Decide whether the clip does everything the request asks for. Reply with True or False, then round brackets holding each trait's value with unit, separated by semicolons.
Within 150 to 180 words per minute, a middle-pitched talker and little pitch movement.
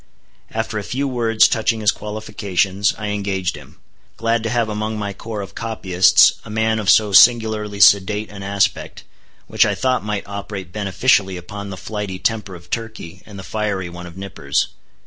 False (175 wpm; 105 Hz; 2.3 semitones)